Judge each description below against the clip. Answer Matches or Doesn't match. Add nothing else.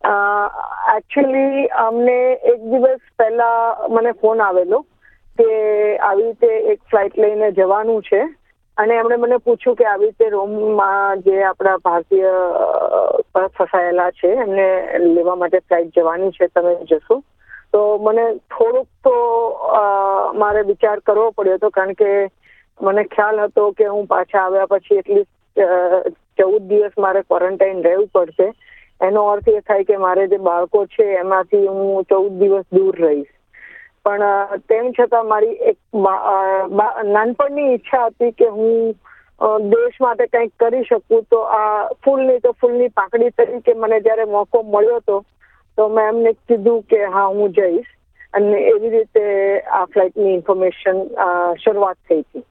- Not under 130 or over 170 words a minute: Matches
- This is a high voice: Matches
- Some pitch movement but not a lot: Matches